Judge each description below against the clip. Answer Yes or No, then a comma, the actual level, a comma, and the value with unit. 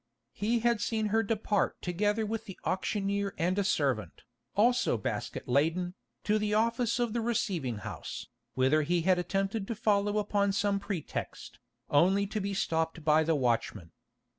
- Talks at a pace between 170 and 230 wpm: No, average, 160 wpm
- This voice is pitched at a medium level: No, high, 200 Hz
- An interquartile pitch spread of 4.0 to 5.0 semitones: Yes, average, 4.6 semitones